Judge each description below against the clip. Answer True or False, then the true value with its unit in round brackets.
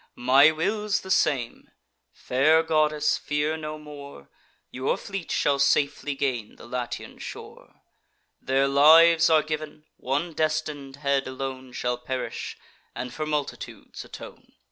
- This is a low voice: False (145 Hz)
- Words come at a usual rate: False (125 wpm)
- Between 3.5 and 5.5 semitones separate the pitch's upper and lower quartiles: False (2.7 semitones)